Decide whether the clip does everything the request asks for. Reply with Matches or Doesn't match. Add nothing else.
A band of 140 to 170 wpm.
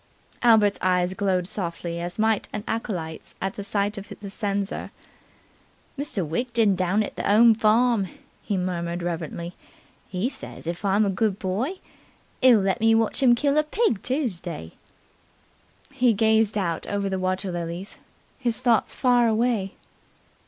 Matches